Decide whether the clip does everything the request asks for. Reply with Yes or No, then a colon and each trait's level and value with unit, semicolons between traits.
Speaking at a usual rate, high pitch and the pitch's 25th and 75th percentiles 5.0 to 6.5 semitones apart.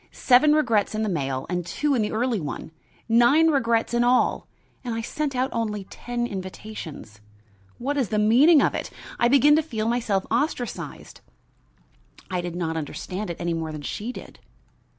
Yes: average, 175 wpm; high, 225 Hz; wide, 5.6 semitones